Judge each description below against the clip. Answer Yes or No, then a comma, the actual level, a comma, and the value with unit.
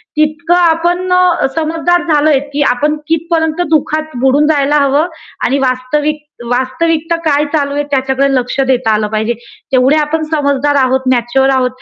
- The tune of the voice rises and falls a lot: No, average, 3.3 semitones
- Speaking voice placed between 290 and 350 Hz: Yes, very high, 295 Hz